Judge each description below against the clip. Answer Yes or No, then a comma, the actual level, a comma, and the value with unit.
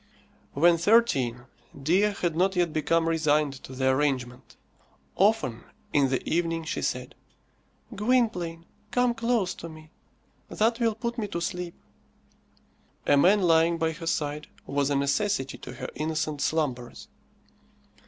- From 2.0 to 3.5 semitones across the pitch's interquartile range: No, average, 5.2 semitones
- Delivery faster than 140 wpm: No, slow, 135 wpm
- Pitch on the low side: No, medium, 165 Hz